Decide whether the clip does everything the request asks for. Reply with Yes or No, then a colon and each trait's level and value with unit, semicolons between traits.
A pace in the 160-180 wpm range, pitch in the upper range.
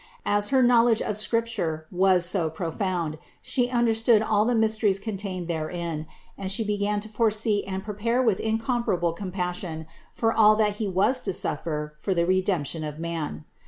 Yes: average, 165 wpm; high, 200 Hz